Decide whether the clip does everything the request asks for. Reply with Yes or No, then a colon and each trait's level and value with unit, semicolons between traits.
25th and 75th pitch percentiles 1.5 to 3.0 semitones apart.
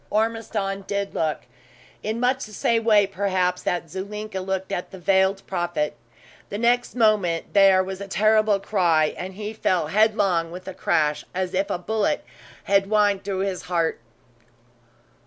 Yes: narrow, 2.6 semitones